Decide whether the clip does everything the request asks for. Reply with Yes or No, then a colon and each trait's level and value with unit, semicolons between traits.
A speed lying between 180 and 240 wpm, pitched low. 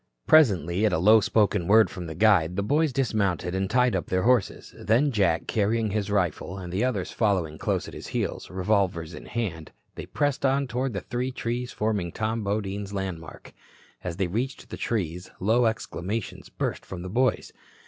Yes: average, 185 wpm; low, 100 Hz